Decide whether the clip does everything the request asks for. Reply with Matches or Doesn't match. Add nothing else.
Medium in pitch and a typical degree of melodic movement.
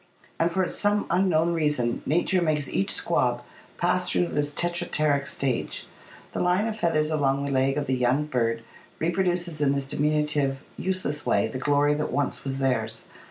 Matches